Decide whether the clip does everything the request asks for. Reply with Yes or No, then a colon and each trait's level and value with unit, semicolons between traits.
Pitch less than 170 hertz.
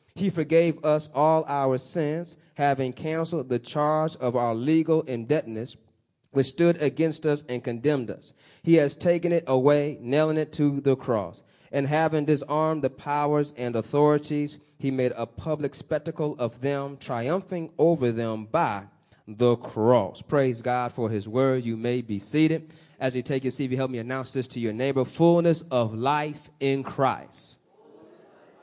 Yes: medium, 140 Hz